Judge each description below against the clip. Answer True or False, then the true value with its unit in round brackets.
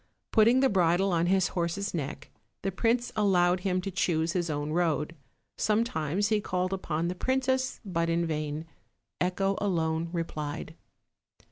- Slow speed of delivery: False (145 wpm)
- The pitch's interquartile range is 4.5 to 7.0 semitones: False (3.3 semitones)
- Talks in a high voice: False (180 Hz)